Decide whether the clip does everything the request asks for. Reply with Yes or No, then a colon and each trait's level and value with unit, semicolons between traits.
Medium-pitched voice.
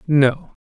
Yes: medium, 145 Hz